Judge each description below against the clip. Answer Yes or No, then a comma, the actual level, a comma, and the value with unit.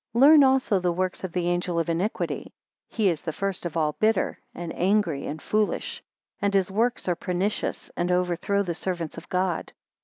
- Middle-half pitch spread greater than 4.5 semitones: No, average, 3.0 semitones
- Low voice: No, medium, 185 Hz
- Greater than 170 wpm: Yes, average, 185 wpm